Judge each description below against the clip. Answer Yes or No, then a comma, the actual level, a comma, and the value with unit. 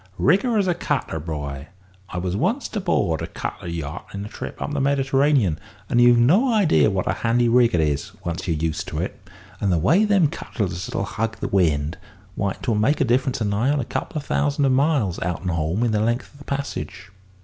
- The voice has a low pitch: Yes, low, 115 Hz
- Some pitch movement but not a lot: No, wide, 8.2 semitones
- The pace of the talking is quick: Yes, fast, 225 wpm